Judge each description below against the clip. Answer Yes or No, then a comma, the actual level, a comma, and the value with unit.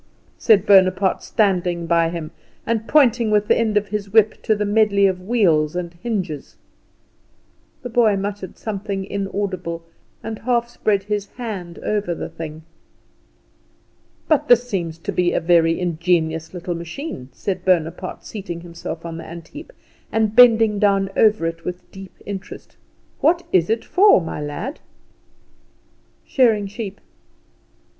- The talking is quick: No, slow, 135 wpm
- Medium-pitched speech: No, high, 195 Hz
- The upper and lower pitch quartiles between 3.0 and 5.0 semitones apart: Yes, average, 4.2 semitones